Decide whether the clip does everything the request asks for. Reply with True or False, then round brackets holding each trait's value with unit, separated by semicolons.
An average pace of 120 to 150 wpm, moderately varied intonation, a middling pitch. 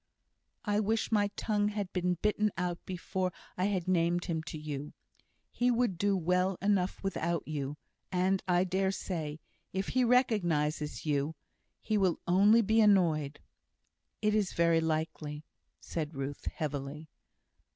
True (140 wpm; 4.3 semitones; 180 Hz)